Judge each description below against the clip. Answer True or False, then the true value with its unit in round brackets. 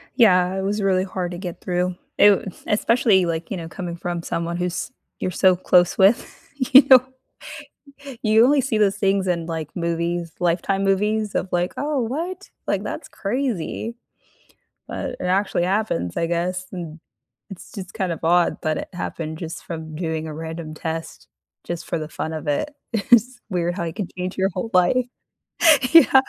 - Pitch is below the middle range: False (180 Hz)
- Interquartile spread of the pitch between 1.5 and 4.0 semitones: True (3.4 semitones)